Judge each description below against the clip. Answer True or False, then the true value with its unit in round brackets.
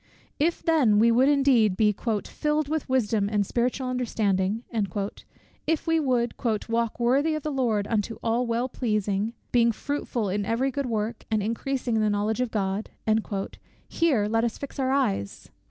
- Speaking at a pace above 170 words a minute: False (165 wpm)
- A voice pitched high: True (235 Hz)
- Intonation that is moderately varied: True (4.0 semitones)